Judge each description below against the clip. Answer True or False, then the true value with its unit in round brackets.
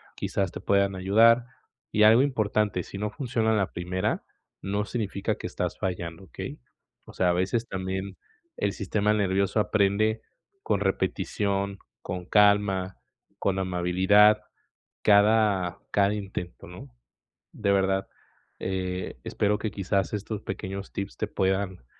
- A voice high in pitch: False (100 Hz)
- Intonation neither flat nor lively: False (1.9 semitones)